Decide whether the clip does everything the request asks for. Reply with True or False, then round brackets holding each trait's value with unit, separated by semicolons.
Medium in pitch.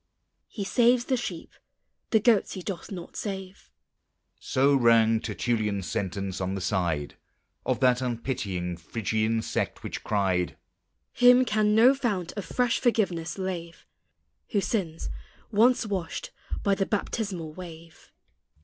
True (170 Hz)